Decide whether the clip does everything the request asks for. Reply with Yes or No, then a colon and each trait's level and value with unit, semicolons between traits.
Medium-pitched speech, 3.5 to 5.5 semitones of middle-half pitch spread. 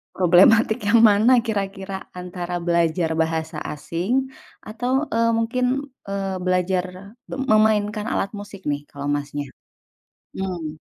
No: high, 195 Hz; average, 4.1 semitones